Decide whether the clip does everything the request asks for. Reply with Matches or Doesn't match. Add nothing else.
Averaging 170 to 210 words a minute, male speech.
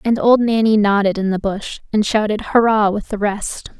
Doesn't match